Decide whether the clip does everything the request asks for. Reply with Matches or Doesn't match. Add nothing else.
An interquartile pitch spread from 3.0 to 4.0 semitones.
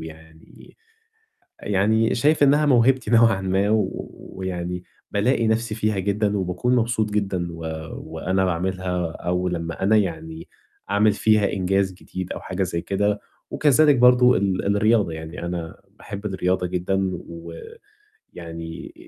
Matches